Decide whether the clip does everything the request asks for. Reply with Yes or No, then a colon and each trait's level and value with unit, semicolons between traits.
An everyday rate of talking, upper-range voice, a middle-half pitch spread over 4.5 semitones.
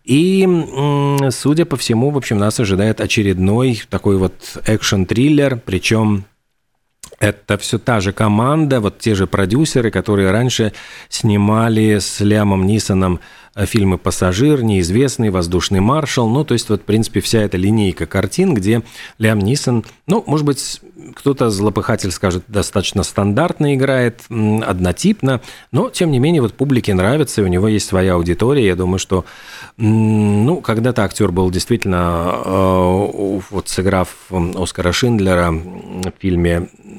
No: average, 135 wpm; low, 105 Hz; average, 4.9 semitones